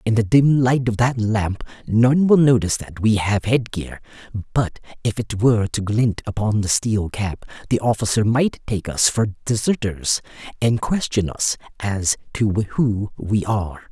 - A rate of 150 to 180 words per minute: Yes, average, 175 wpm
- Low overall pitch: Yes, low, 110 Hz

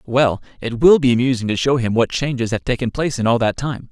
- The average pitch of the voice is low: Yes, low, 120 Hz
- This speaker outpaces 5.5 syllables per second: Yes, 6.0 syllables/s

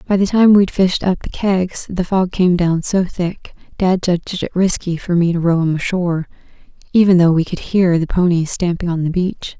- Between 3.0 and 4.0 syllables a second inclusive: No, 4.9 syllables/s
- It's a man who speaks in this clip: No, female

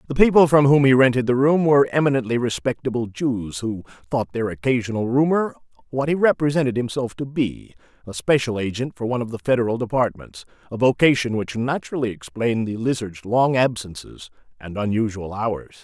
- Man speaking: Yes, male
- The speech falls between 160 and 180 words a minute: Yes, average, 165 wpm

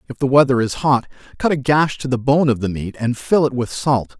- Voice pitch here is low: Yes, low, 130 Hz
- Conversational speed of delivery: No, fast, 270 wpm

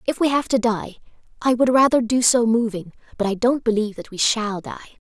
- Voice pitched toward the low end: No, high, 230 Hz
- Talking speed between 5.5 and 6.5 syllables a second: Yes, 5.8 syllables/s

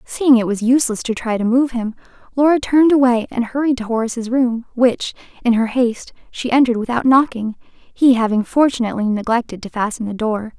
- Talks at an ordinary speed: Yes, average, 185 wpm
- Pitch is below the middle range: No, high, 240 Hz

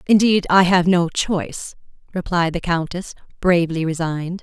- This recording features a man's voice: No, female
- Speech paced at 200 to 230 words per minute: No, slow, 135 wpm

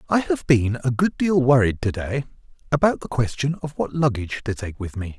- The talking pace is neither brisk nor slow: No, fast, 220 wpm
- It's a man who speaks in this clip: Yes, male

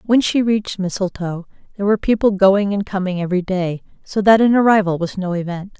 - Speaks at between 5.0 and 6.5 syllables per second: Yes, 6.0 syllables/s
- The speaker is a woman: Yes, female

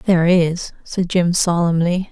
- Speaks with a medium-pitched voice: Yes, medium, 175 Hz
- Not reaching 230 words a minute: Yes, average, 140 wpm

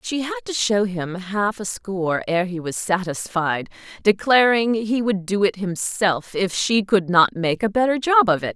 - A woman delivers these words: Yes, female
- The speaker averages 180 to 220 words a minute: Yes, average, 195 wpm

